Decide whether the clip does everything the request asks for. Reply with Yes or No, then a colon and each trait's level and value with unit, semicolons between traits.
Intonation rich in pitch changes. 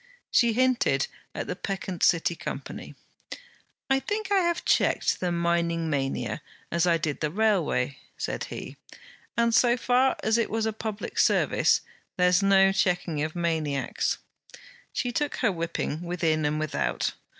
Yes: wide, 5.9 semitones